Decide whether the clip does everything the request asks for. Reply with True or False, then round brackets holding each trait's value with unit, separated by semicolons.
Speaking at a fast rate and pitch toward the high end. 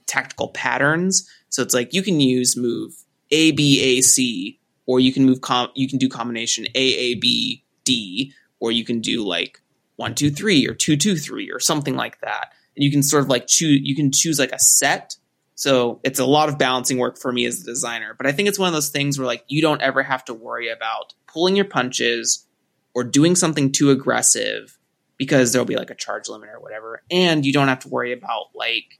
False (225 wpm; 135 Hz)